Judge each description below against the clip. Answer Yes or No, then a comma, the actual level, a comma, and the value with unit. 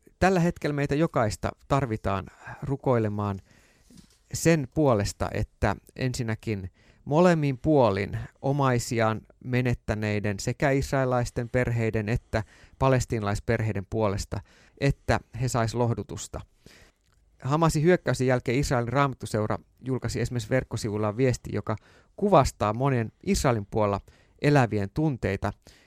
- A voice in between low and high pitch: No, low, 120 Hz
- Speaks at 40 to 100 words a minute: Yes, slow, 95 wpm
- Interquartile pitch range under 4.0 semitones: No, average, 4.4 semitones